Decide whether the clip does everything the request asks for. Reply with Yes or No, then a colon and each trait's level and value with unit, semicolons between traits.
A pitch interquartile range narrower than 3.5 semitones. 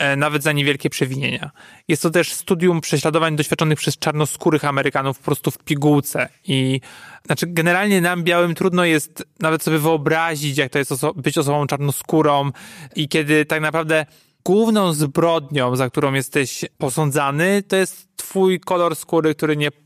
Yes: average, 2.8 semitones